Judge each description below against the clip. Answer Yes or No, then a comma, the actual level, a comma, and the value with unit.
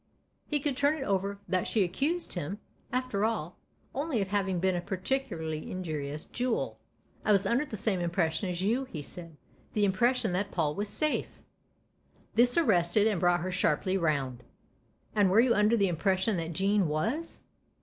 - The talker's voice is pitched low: No, high, 195 Hz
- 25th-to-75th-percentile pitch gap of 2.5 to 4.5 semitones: No, average, 5.0 semitones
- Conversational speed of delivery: Yes, average, 180 wpm